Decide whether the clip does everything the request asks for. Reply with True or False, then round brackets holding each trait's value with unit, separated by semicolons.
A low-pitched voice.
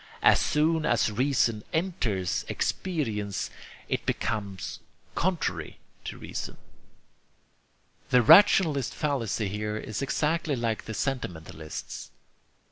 True (120 Hz)